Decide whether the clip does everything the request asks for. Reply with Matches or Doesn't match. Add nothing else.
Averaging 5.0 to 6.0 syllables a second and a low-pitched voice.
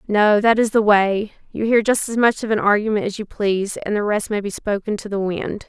Doesn't match